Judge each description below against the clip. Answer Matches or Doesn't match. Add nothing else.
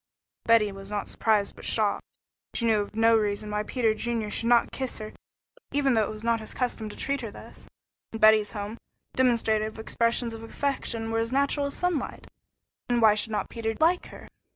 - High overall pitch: Matches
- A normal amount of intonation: Doesn't match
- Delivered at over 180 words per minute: Matches